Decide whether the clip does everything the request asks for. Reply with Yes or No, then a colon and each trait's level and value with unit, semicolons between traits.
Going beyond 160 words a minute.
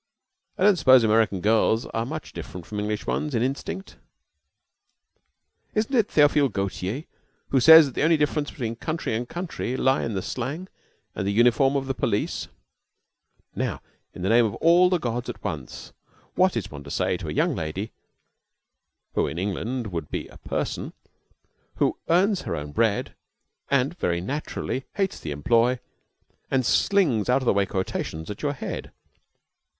Yes: average, 170 wpm